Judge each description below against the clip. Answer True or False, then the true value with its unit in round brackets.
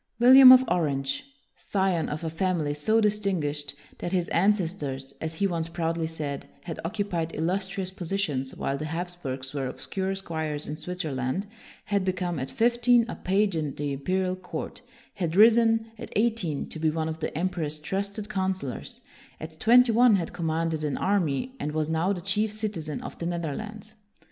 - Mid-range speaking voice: True (175 Hz)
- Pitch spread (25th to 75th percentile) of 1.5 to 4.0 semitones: False (4.5 semitones)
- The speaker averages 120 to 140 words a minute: False (170 wpm)